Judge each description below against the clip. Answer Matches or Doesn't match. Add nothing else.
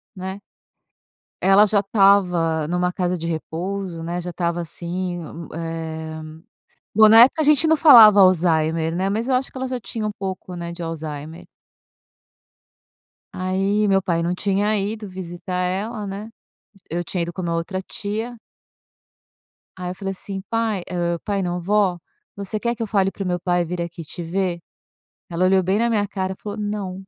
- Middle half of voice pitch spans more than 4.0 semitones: Doesn't match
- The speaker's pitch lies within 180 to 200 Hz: Matches